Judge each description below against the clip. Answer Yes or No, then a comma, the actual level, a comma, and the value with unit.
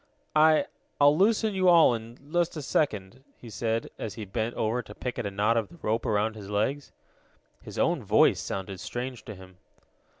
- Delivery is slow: No, average, 195 wpm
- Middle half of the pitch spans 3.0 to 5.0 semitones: No, wide, 5.6 semitones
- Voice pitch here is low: Yes, low, 115 Hz